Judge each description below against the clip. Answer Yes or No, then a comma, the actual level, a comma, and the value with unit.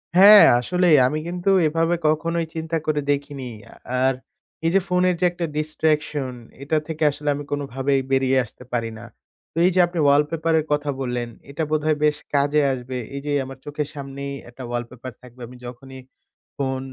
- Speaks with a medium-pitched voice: Yes, medium, 145 Hz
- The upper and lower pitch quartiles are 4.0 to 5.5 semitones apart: No, average, 3.4 semitones